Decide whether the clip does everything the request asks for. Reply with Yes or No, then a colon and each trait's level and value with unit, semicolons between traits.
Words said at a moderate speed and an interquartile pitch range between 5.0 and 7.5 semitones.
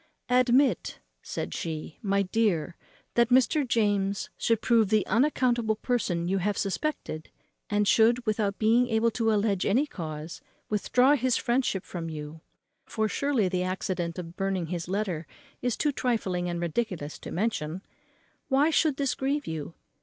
Yes: average, 150 wpm; wide, 5.4 semitones